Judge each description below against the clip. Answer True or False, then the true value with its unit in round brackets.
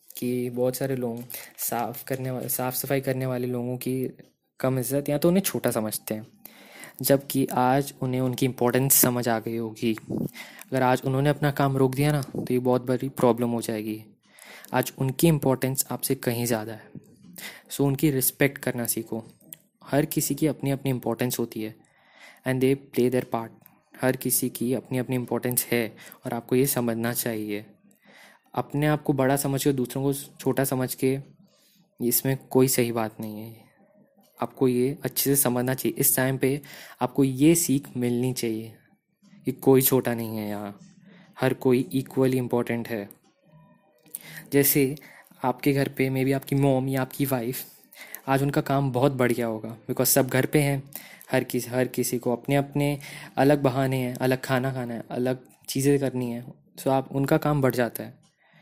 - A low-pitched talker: True (130 Hz)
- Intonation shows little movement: True (2.3 semitones)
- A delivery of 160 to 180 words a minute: True (175 wpm)